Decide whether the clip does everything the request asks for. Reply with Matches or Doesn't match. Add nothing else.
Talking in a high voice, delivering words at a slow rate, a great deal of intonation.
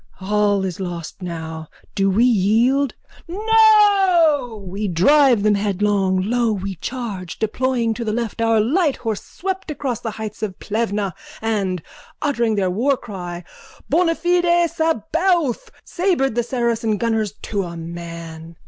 Matches